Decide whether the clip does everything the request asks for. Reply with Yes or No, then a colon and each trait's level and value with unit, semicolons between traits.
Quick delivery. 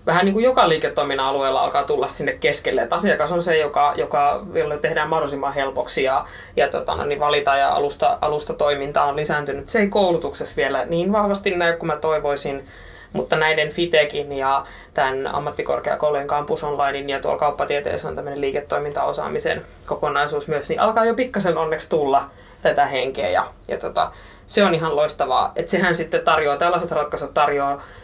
Yes: fast, 165 wpm